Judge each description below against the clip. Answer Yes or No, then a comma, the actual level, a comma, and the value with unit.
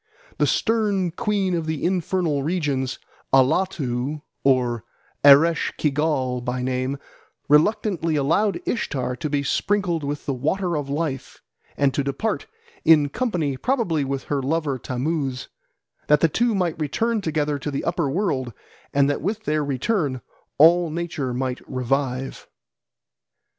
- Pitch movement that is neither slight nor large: Yes, average, 4.4 semitones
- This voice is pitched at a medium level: Yes, medium, 150 Hz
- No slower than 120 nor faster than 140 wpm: Yes, slow, 135 wpm